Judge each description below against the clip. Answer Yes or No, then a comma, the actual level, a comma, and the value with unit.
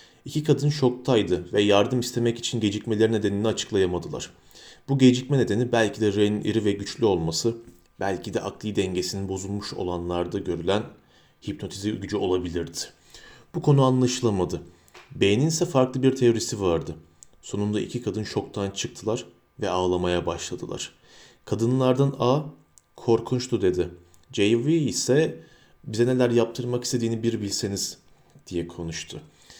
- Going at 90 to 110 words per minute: No, average, 125 wpm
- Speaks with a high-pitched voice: No, low, 110 Hz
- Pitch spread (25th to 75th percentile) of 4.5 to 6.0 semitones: No, average, 4.1 semitones